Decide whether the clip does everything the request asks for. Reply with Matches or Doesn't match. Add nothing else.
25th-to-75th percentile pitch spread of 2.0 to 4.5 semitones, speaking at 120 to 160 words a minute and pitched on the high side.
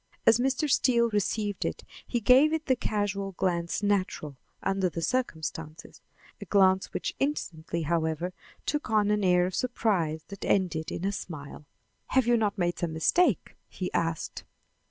Doesn't match